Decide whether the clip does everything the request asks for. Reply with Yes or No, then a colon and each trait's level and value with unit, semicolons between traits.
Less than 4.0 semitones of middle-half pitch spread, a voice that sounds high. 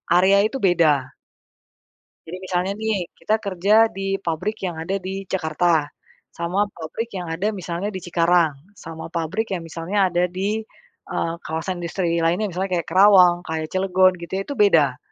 No: average, 2.8 semitones; medium, 180 Hz